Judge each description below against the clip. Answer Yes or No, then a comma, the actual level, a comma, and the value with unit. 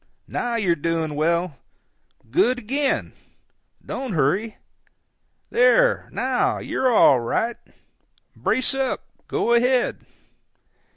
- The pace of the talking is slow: Yes, slow, 70 wpm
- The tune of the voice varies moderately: No, wide, 7.2 semitones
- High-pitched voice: Yes, high, 230 Hz